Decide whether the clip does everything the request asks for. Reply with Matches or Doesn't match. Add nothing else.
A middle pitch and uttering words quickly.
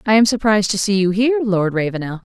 Doesn't match